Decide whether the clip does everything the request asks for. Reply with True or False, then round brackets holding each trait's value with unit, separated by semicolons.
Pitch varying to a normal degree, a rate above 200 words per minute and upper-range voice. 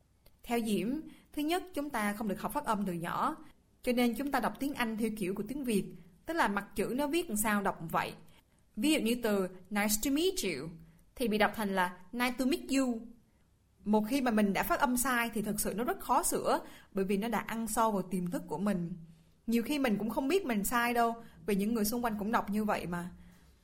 True (4.3 semitones; 250 wpm; 220 Hz)